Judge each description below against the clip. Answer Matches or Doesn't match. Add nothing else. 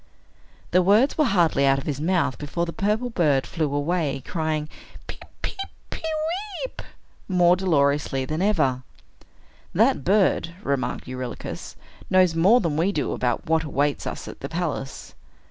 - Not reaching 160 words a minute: Matches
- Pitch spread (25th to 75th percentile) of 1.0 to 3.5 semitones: Doesn't match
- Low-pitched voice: Doesn't match